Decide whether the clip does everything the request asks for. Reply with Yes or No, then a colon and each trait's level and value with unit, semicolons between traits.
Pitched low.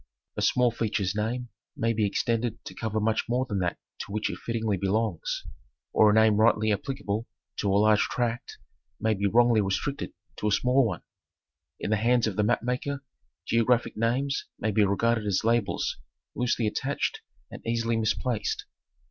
Yes: low, 110 Hz